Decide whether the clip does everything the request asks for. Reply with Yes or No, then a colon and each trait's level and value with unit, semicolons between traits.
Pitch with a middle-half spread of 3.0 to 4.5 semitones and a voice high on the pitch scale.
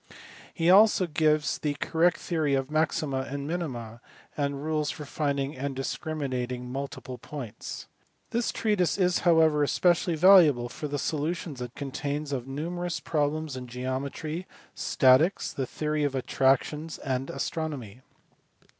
No: average, 3.3 semitones; medium, 145 Hz